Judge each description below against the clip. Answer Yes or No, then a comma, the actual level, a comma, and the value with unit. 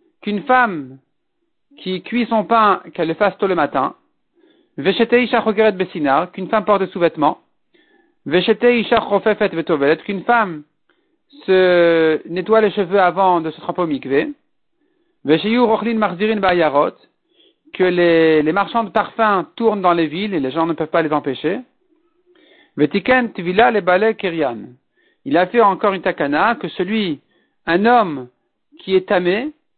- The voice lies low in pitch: No, high, 205 Hz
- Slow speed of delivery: Yes, slow, 120 wpm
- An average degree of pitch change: No, wide, 6.3 semitones